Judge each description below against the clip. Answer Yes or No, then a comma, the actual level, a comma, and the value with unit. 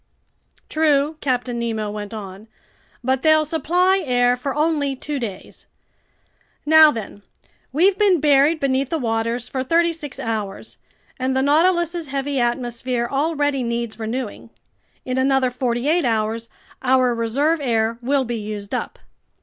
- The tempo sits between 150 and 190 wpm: No, average, 140 wpm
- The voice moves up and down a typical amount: Yes, average, 4.3 semitones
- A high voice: Yes, very high, 260 Hz